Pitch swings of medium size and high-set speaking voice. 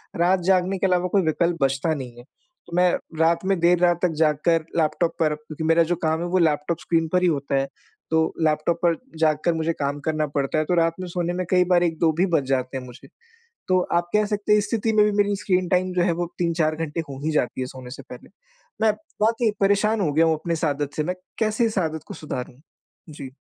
No: average, 3.0 semitones; medium, 165 Hz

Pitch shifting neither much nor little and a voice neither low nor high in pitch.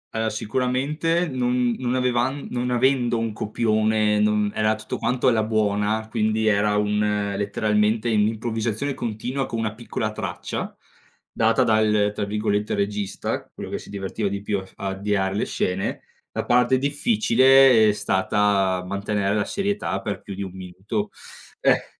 No: average, 3.0 semitones; low, 110 Hz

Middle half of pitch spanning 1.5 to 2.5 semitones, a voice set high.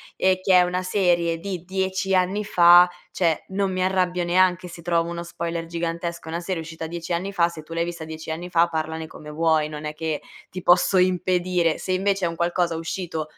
No: narrow, 1.8 semitones; medium, 175 Hz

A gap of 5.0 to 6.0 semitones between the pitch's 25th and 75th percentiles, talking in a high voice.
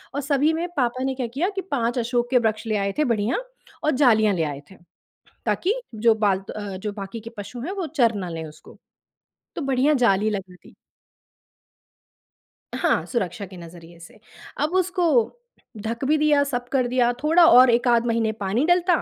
Yes: wide, 5.4 semitones; high, 235 Hz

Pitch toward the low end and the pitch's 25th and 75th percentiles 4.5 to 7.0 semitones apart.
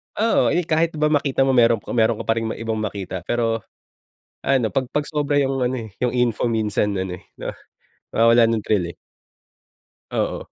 No: low, 120 Hz; average, 3.6 semitones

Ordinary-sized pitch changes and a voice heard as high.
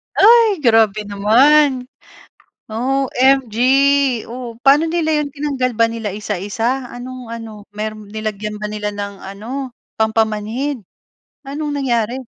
Yes: average, 4.2 semitones; high, 235 Hz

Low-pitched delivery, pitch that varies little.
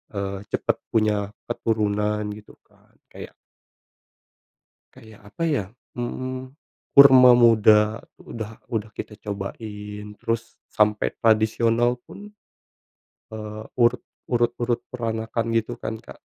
Yes: low, 110 Hz; narrow, 1.8 semitones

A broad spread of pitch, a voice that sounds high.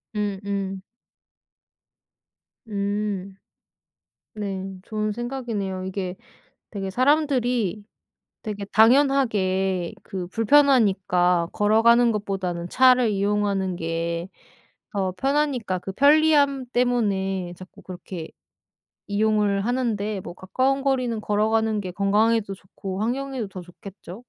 No: average, 4.1 semitones; high, 205 Hz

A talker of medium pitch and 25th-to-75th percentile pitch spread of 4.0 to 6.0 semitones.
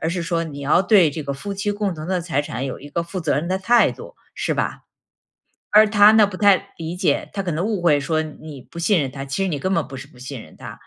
Yes: medium, 170 Hz; average, 5.2 semitones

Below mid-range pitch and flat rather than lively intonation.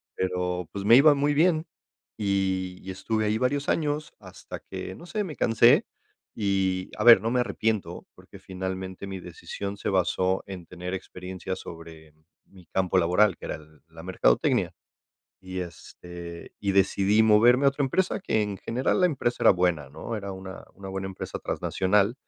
No: very low, 95 Hz; average, 3.6 semitones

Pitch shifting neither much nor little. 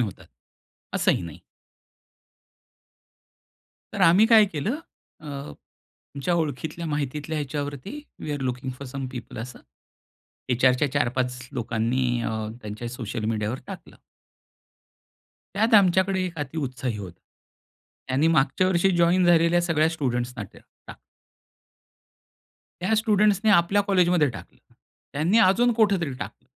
No: wide, 6.5 semitones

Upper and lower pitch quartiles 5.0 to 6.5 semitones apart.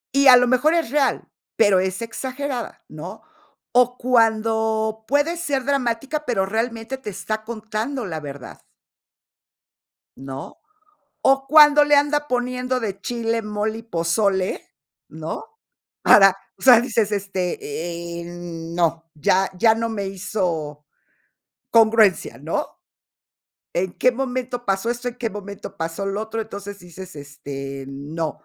Yes: wide, 5.5 semitones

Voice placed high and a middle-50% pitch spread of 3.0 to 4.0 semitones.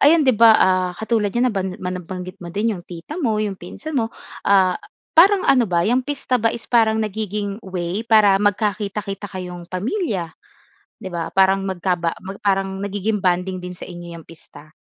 Yes: high, 195 Hz; average, 3.3 semitones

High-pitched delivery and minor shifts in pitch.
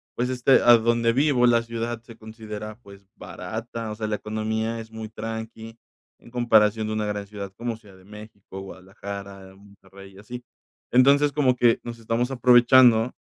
No: low, 110 Hz; narrow, 2.3 semitones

